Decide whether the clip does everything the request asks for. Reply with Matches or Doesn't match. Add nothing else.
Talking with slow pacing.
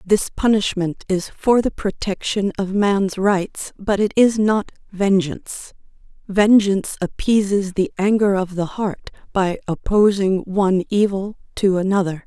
Matches